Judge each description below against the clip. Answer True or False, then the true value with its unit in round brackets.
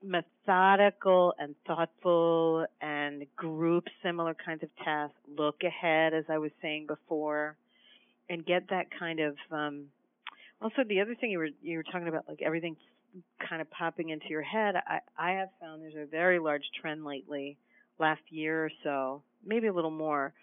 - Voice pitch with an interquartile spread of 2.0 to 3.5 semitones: True (2.6 semitones)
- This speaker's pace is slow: False (170 wpm)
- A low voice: False (160 Hz)